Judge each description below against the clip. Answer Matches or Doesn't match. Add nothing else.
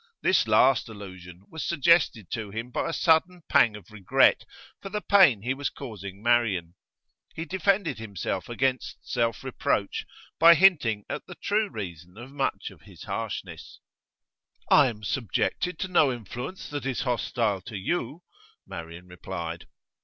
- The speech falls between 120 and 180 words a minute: Matches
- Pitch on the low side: Matches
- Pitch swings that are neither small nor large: Doesn't match